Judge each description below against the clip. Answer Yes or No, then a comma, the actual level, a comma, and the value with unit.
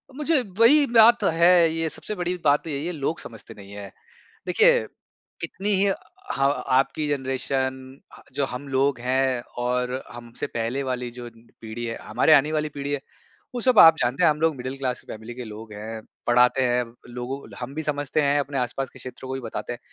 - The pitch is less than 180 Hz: Yes, low, 135 Hz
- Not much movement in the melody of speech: No, average, 3.7 semitones